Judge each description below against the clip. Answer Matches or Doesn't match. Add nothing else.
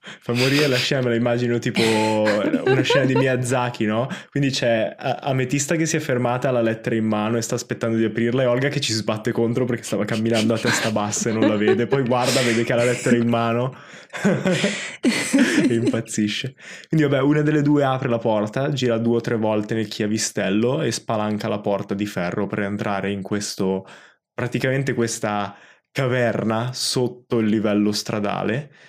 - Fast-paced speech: Matches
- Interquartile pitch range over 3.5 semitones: Doesn't match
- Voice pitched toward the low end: Matches